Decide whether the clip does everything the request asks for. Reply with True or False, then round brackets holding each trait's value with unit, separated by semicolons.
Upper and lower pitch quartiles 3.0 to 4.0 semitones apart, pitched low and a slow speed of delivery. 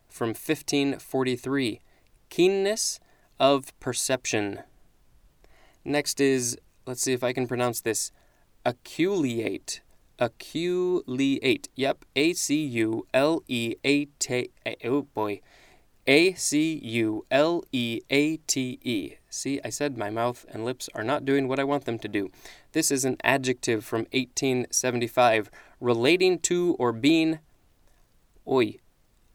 True (3.7 semitones; 130 Hz; 125 wpm)